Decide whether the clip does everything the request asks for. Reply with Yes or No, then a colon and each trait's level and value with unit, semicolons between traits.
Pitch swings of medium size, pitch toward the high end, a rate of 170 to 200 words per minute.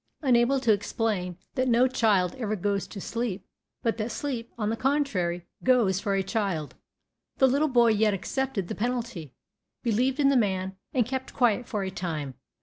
Yes: average, 4.7 semitones; high, 225 Hz; average, 175 wpm